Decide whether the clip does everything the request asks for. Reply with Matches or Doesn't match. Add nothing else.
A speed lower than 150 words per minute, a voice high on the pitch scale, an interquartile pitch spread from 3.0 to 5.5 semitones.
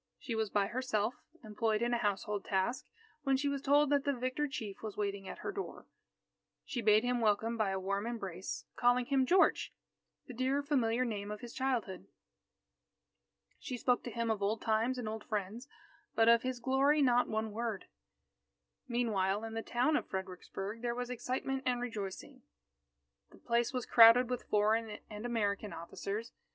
Doesn't match